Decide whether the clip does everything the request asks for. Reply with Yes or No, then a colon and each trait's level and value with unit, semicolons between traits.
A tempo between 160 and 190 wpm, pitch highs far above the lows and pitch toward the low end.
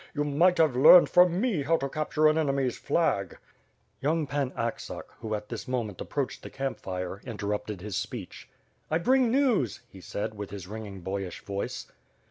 Yes: average, 175 wpm; wide, 7.4 semitones; low, 130 Hz